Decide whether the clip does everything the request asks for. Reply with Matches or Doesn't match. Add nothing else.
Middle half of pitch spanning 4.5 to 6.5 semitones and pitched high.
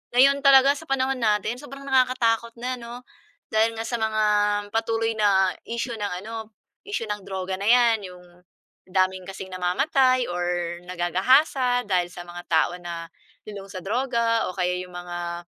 Matches